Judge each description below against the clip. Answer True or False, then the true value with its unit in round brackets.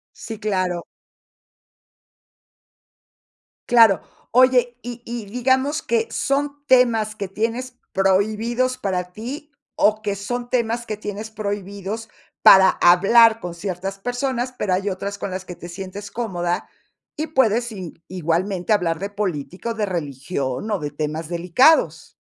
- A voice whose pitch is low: False (210 Hz)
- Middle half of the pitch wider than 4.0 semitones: True (4.5 semitones)